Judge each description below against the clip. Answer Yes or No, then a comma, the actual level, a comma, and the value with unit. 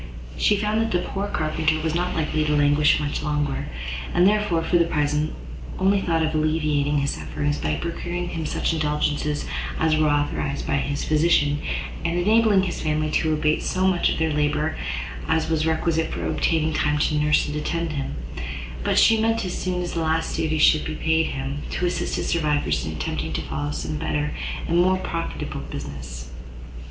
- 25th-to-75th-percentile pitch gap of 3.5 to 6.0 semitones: No, narrow, 2.6 semitones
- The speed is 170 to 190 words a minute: Yes, average, 185 wpm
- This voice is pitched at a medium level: Yes, medium, 155 Hz